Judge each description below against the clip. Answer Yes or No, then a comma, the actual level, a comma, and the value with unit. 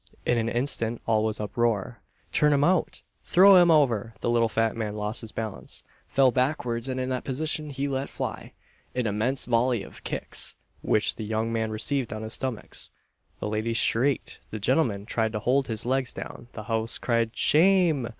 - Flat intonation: No, average, 3.4 semitones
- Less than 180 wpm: No, average, 185 wpm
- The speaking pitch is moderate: No, low, 120 Hz